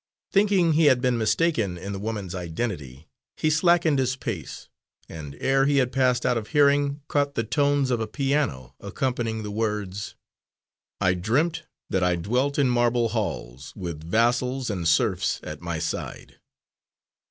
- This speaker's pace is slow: No, average, 165 wpm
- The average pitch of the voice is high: No, low, 115 Hz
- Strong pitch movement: Yes, wide, 7.2 semitones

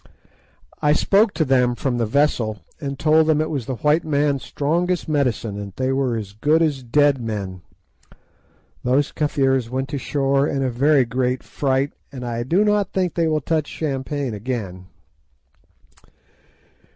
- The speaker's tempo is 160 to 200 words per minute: Yes, average, 170 wpm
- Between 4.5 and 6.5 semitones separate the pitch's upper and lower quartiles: No, average, 3.6 semitones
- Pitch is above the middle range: No, low, 135 Hz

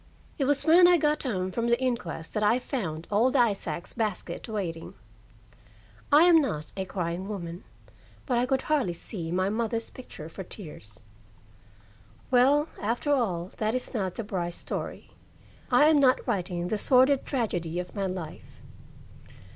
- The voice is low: No, high, 215 Hz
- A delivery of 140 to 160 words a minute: Yes, average, 155 wpm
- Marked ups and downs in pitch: Yes, wide, 6.4 semitones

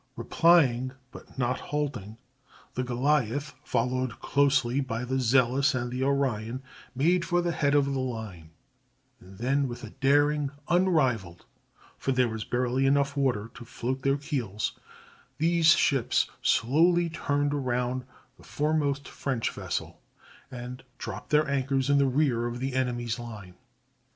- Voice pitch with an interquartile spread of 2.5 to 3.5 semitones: Yes, average, 2.9 semitones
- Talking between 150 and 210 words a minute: No, average, 140 wpm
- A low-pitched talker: Yes, low, 130 Hz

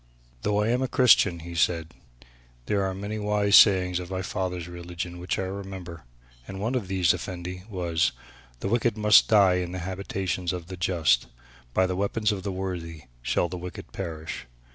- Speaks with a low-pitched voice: Yes, very low, 95 Hz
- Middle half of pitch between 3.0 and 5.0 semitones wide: No, narrow, 2.5 semitones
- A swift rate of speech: No, average, 185 wpm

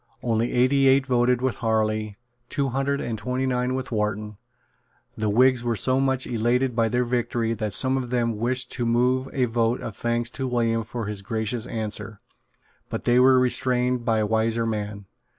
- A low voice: Yes, low, 120 Hz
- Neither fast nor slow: Yes, average, 180 wpm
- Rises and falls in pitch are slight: Yes, narrow, 2.3 semitones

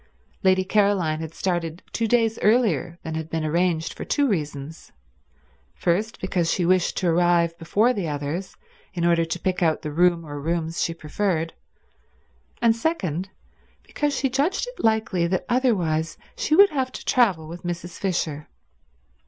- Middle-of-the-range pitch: Yes, medium, 175 Hz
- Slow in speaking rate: No, average, 160 wpm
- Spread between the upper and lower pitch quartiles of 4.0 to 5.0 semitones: Yes, average, 4.7 semitones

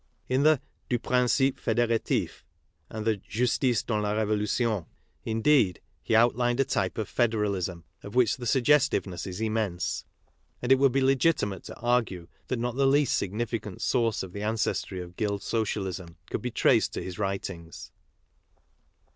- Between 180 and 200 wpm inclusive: No, average, 155 wpm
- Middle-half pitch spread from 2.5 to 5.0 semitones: Yes, average, 3.8 semitones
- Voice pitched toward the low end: Yes, low, 110 Hz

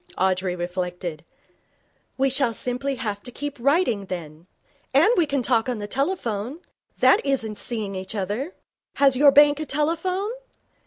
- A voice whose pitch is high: Yes, high, 245 Hz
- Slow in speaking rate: No, average, 150 wpm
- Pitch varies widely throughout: Yes, wide, 6.4 semitones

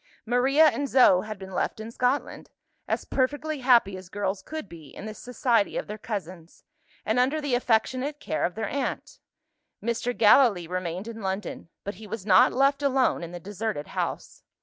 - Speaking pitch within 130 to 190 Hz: No, high, 220 Hz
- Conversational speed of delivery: Yes, average, 180 wpm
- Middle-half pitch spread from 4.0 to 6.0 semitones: Yes, average, 5.2 semitones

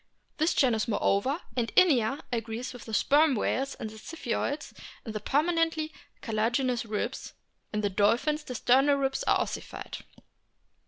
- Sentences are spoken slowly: No, average, 150 wpm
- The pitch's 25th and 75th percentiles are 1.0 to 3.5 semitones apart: No, average, 4.8 semitones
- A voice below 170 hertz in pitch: No, very high, 250 Hz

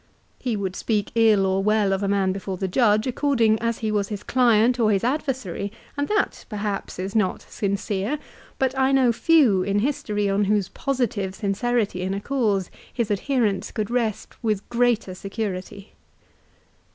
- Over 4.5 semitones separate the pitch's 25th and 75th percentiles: No, average, 3.5 semitones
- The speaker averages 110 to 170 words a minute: Yes, average, 165 wpm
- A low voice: No, high, 210 Hz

